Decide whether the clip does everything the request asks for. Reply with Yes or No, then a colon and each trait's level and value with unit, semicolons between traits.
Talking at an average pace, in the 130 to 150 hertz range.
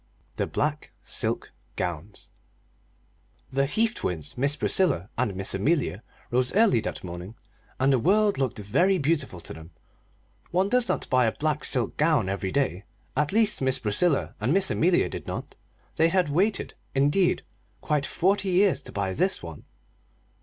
Yes: average, 160 wpm; medium, 140 Hz